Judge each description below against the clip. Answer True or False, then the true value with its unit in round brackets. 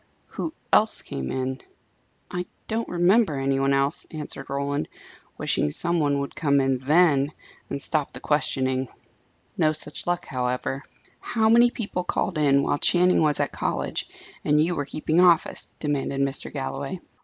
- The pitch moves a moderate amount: True (4.2 semitones)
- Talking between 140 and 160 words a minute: True (155 wpm)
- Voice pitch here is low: False (145 Hz)